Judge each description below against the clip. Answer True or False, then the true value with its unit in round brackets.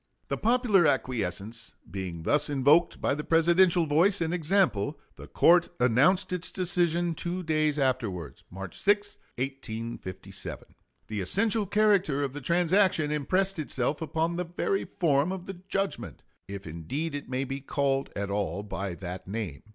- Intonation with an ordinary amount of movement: False (7.1 semitones)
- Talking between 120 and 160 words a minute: True (150 wpm)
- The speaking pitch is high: False (150 Hz)